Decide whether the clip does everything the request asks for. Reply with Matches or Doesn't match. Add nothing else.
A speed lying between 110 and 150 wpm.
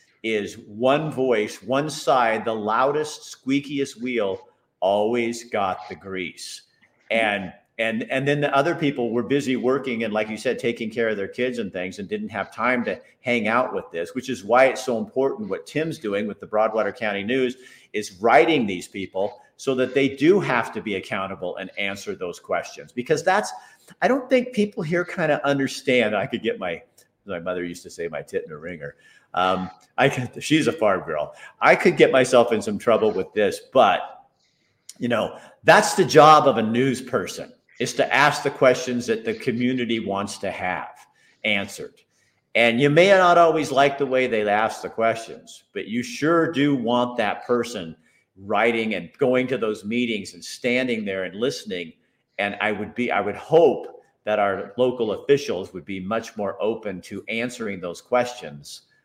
Doesn't match